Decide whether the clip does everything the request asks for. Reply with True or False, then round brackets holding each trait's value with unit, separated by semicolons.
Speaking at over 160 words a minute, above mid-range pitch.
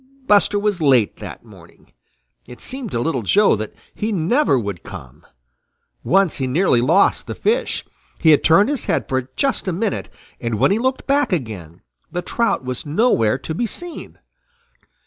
False (170 wpm; 170 Hz)